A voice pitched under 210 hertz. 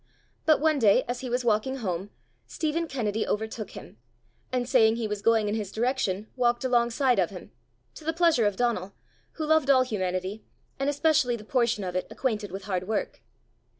No: high, 235 Hz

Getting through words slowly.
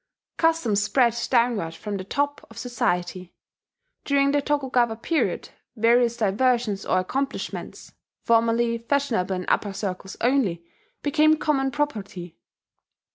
Yes: slow, 115 wpm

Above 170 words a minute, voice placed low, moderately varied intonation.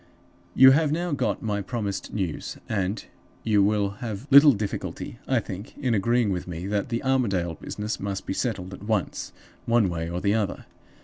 Yes: average, 180 wpm; low, 105 Hz; average, 3.7 semitones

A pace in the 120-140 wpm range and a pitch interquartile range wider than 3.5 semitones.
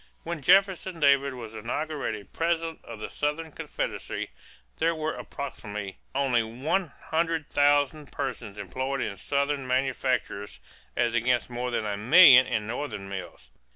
Yes: slow, 135 wpm; average, 5.2 semitones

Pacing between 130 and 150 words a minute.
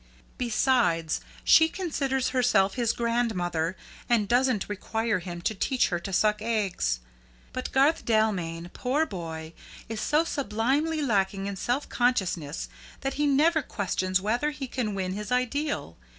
Yes: average, 140 wpm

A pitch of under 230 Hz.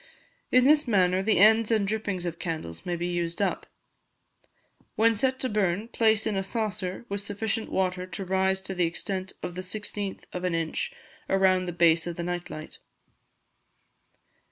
Yes: high, 190 Hz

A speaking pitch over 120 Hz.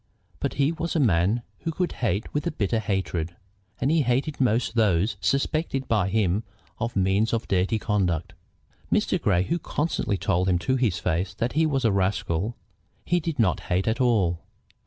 No: low, 110 Hz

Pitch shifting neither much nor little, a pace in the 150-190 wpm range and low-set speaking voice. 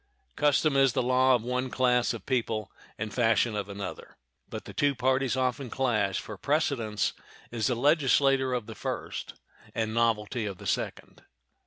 Yes: average, 3.2 semitones; average, 165 wpm; low, 125 Hz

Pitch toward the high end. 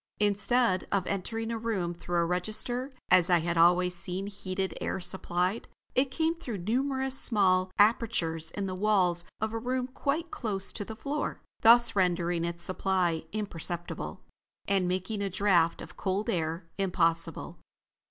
Yes: high, 195 Hz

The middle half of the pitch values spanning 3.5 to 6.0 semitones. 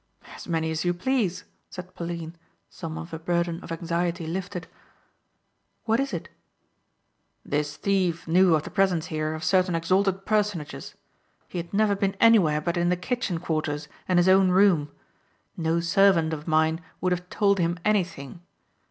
No: average, 2.9 semitones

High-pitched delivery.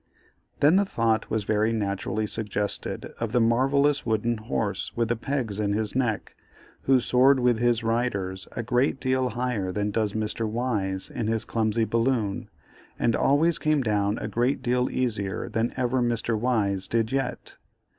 No: low, 115 Hz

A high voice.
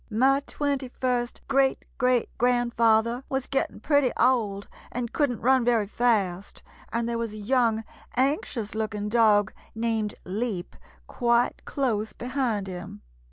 Yes: high, 235 Hz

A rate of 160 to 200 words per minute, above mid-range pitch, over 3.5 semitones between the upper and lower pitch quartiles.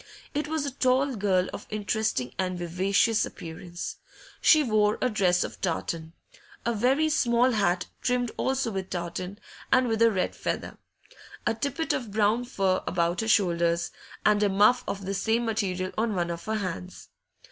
Yes: average, 170 wpm; high, 210 Hz; average, 4.7 semitones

